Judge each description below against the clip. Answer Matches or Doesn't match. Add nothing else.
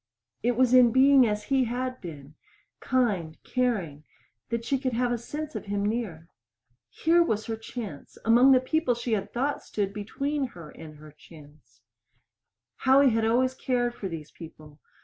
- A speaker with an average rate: Matches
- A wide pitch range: Matches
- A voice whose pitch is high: Matches